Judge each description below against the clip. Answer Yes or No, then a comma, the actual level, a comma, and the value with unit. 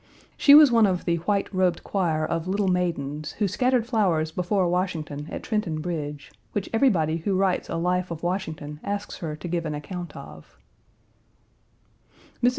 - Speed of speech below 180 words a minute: Yes, average, 165 wpm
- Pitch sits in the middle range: Yes, medium, 180 Hz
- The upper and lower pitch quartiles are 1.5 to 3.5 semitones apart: No, average, 4.0 semitones